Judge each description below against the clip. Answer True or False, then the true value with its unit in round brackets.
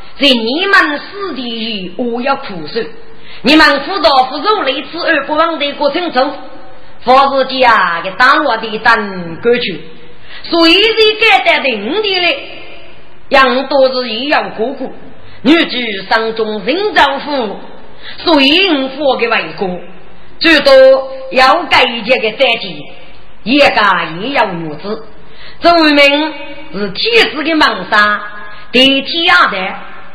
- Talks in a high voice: True (265 Hz)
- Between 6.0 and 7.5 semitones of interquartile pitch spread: False (5.4 semitones)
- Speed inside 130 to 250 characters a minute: True (185 characters per minute)